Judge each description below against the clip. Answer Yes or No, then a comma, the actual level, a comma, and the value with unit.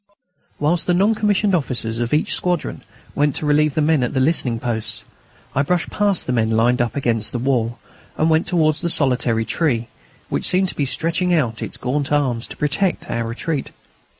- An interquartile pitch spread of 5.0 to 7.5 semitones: Yes, wide, 5.6 semitones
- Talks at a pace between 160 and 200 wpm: Yes, average, 195 wpm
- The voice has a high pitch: No, medium, 145 Hz